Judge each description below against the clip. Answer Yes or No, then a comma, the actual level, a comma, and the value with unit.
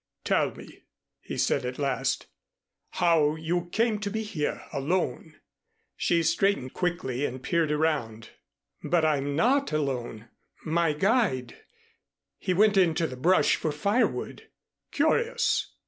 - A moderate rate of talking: No, slow, 125 wpm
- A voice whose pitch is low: No, medium, 160 Hz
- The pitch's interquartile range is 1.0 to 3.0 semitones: No, average, 5.0 semitones